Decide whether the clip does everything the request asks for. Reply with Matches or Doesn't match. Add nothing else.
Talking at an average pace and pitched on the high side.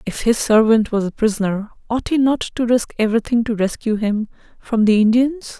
Matches